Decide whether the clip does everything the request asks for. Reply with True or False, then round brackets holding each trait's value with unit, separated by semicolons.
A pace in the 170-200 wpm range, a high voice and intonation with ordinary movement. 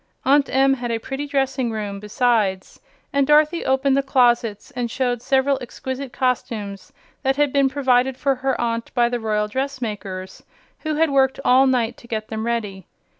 True (175 wpm; 250 Hz; 3.1 semitones)